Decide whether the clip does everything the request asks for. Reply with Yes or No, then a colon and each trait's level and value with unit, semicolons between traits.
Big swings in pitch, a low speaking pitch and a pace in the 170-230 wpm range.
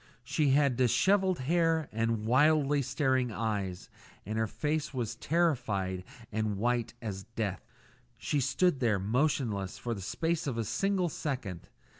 No: wide, 5.8 semitones; low, 125 Hz; average, 140 wpm